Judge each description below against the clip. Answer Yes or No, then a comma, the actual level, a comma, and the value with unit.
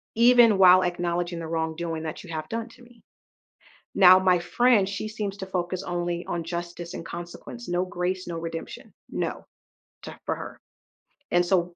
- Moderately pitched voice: Yes, medium, 175 Hz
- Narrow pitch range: Yes, narrow, 2.2 semitones